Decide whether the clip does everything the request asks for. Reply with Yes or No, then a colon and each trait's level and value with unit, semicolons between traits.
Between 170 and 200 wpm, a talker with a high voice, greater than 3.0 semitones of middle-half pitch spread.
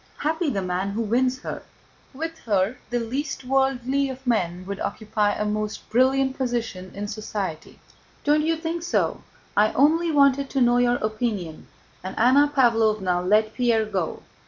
No: average, 160 wpm; high, 240 Hz; average, 4.4 semitones